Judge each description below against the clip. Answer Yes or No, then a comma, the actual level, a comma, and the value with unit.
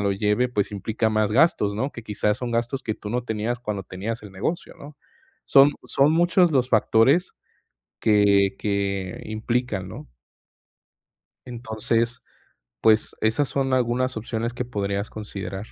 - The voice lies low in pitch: Yes, low, 110 Hz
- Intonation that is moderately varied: Yes, average, 3.3 semitones